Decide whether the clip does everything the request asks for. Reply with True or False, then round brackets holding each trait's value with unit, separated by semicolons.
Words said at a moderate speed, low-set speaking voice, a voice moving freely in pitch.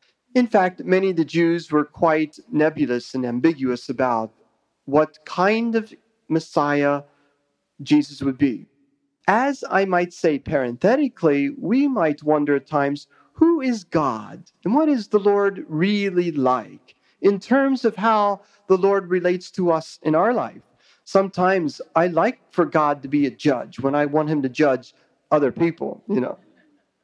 False (155 wpm; 170 Hz; 5.8 semitones)